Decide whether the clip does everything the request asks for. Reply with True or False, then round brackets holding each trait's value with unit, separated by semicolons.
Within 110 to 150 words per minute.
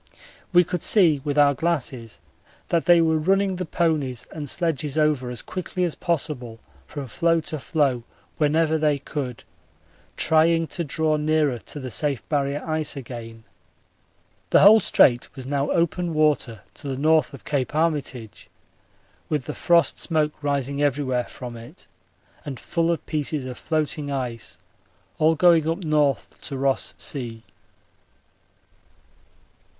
True (145 wpm)